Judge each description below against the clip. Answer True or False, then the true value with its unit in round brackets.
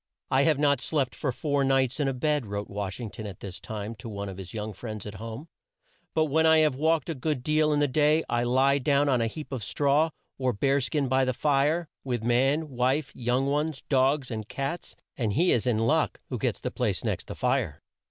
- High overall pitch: False (135 Hz)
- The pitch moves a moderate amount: True (4.2 semitones)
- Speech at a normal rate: False (235 wpm)